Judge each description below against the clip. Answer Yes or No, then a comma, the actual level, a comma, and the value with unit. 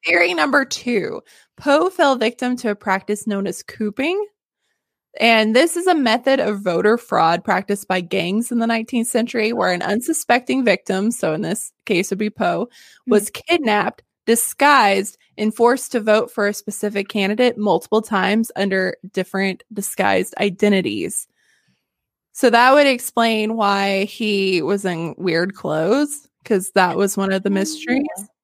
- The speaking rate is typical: Yes, average, 155 wpm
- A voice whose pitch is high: Yes, high, 215 Hz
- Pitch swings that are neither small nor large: Yes, average, 3.6 semitones